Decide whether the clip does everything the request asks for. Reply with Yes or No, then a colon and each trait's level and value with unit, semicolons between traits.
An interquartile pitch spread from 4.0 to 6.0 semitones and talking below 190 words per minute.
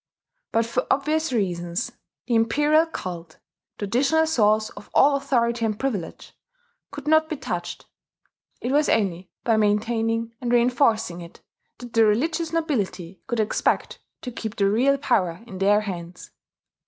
Yes: average, 5.2 semitones; average, 140 wpm